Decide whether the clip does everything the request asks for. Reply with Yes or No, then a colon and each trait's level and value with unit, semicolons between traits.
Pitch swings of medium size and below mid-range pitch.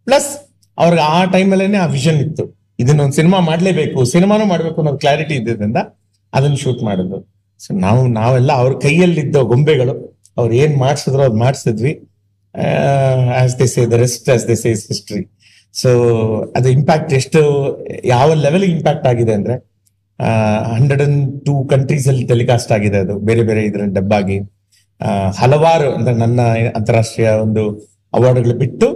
Yes: average, 4.9 semitones; low, 125 Hz